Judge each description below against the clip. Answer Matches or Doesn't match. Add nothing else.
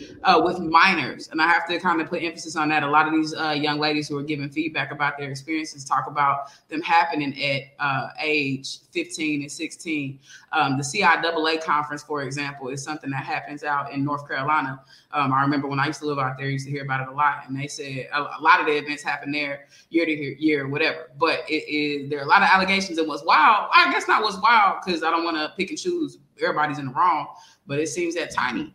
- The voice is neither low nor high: Matches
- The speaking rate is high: Matches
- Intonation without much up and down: Matches